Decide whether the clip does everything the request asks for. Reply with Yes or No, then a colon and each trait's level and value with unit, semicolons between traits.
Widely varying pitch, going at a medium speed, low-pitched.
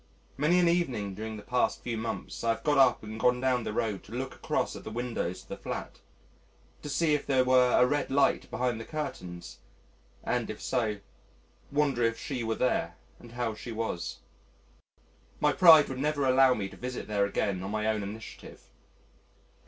No: average, 3.7 semitones; average, 190 wpm; low, 120 Hz